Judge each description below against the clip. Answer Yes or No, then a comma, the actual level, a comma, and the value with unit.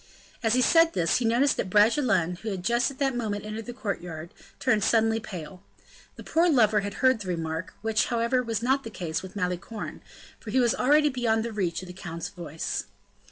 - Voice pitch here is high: Yes, high, 220 Hz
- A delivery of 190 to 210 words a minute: Yes, fast, 205 wpm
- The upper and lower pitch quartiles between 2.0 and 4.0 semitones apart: No, average, 5.1 semitones